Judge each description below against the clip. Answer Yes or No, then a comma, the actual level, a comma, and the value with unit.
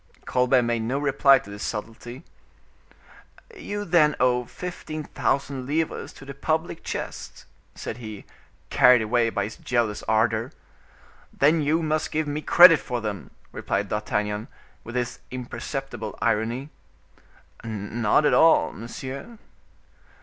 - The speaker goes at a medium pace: No, slow, 130 wpm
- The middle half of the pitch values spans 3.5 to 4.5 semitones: No, average, 5.0 semitones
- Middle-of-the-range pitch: No, low, 125 Hz